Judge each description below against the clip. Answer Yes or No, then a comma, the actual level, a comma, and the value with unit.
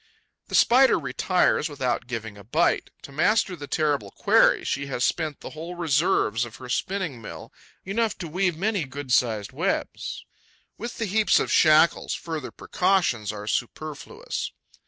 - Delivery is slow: No, average, 155 wpm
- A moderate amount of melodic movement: No, wide, 6.9 semitones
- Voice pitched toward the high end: No, medium, 155 Hz